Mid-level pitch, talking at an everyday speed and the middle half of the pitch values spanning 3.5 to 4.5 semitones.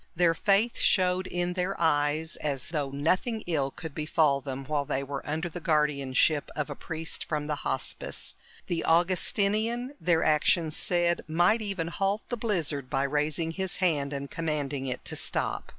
Yes: medium, 160 Hz; average, 165 wpm; average, 3.8 semitones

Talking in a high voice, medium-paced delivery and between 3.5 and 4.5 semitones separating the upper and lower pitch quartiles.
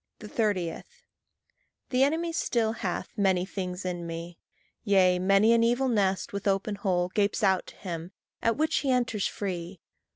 Yes: high, 200 Hz; average, 155 wpm; average, 4.0 semitones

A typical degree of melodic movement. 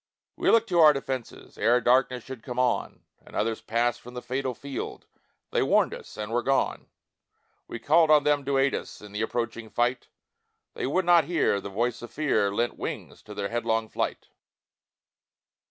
Yes: average, 3.4 semitones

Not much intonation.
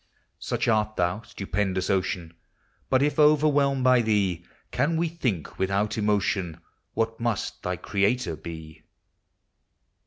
No: average, 5.3 semitones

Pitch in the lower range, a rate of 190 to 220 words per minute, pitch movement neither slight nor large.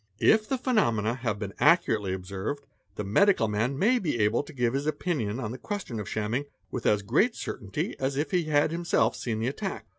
No: low, 125 Hz; fast, 205 wpm; wide, 7.2 semitones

